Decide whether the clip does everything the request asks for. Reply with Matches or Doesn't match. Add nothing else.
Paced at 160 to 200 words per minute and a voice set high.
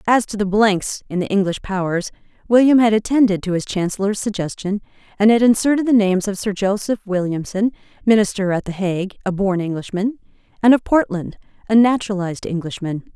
Matches